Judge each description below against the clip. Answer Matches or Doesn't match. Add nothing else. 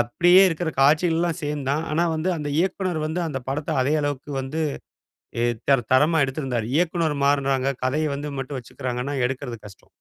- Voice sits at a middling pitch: Matches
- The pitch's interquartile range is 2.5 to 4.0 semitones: Matches